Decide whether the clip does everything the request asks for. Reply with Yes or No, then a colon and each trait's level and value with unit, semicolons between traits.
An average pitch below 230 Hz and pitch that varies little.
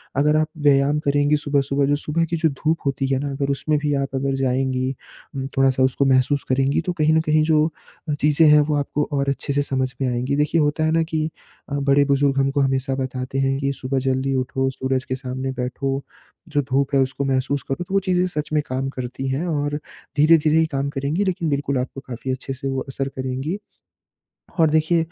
Yes: medium, 140 Hz; narrow, 2.1 semitones